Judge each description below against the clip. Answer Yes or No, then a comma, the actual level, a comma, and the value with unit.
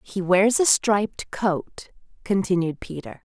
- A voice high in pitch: Yes, high, 195 Hz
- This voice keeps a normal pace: No, slow, 125 wpm